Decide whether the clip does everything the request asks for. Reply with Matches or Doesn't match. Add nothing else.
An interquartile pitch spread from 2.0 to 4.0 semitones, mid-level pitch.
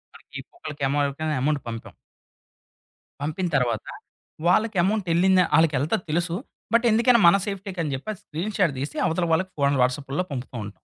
Doesn't match